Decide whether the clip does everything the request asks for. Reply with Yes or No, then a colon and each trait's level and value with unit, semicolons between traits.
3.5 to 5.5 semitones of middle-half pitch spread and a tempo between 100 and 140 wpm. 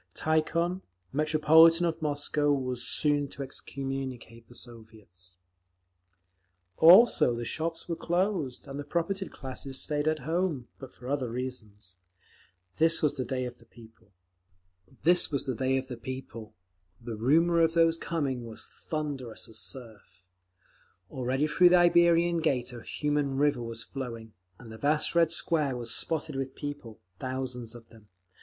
Yes: average, 5.0 semitones; slow, 135 wpm